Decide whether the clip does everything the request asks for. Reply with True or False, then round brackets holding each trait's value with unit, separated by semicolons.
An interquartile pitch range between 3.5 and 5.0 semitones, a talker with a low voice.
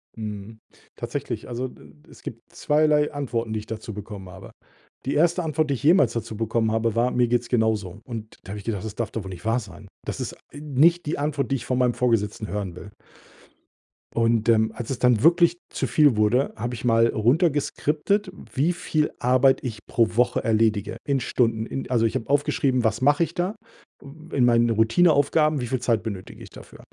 True (4.5 semitones; 120 Hz)